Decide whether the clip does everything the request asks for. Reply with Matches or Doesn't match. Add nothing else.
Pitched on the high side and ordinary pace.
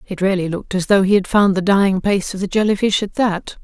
Doesn't match